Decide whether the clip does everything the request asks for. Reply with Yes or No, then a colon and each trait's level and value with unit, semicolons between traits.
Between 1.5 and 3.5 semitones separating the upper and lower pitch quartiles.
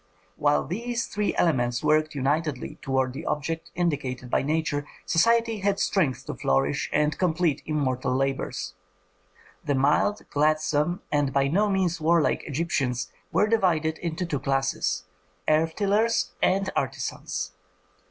No: average, 4.5 semitones